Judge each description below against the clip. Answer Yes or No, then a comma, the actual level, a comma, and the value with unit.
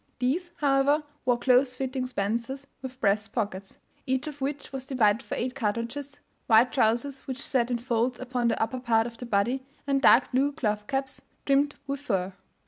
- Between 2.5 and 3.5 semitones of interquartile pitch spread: Yes, average, 2.8 semitones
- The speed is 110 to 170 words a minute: No, average, 180 wpm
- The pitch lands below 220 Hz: No, very high, 255 Hz